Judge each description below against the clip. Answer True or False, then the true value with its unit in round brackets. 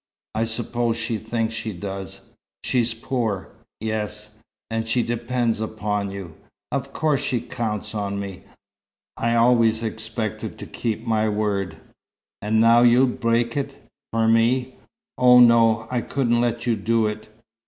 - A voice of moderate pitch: False (115 Hz)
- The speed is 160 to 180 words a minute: False (145 wpm)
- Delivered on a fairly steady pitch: True (1.8 semitones)